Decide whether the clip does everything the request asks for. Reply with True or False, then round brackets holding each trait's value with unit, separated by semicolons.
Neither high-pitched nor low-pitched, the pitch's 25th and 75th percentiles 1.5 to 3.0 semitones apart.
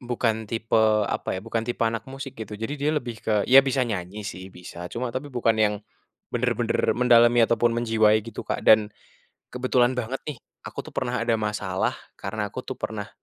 False (115 Hz; 2.6 semitones)